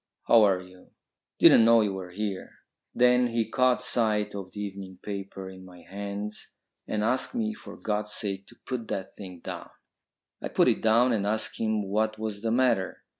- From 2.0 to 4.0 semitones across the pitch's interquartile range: Yes, average, 2.9 semitones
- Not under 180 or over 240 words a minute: Yes, average, 185 wpm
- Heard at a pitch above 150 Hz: No, low, 105 Hz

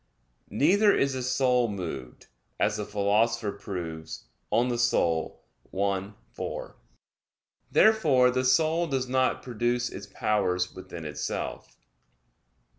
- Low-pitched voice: Yes, low, 115 Hz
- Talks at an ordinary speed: No, slow, 110 wpm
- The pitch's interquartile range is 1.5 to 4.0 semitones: No, average, 4.8 semitones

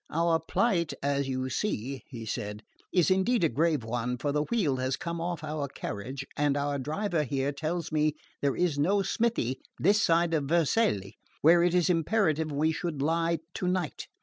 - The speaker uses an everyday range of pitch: Yes, average, 3.8 semitones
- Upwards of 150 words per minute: Yes, average, 175 wpm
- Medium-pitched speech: Yes, medium, 155 Hz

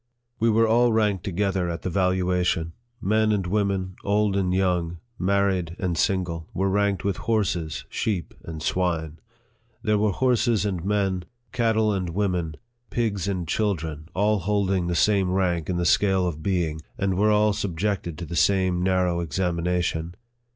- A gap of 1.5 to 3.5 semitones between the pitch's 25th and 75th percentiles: Yes, average, 2.8 semitones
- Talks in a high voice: No, very low, 95 Hz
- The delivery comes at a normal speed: Yes, average, 160 wpm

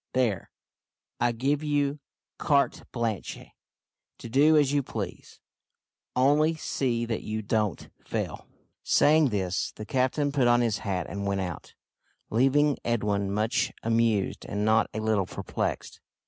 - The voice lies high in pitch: No, low, 115 Hz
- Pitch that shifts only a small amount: No, average, 4.9 semitones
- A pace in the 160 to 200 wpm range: No, slow, 135 wpm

